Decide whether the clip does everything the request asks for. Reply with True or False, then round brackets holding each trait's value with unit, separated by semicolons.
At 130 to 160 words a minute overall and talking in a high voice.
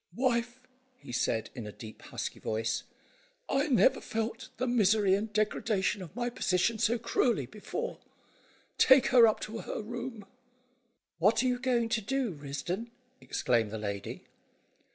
True (150 wpm; 220 Hz)